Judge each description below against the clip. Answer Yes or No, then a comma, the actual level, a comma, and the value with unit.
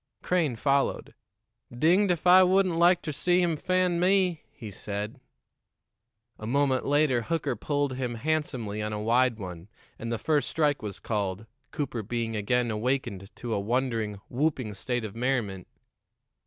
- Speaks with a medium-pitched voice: No, low, 125 Hz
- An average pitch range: No, wide, 6.3 semitones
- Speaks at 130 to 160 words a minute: Yes, average, 155 wpm